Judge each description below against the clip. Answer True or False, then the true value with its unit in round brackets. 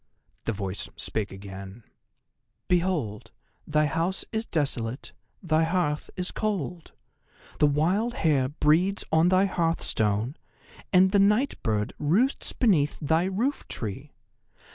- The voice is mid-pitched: True (160 Hz)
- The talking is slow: True (120 wpm)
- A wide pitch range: True (6.7 semitones)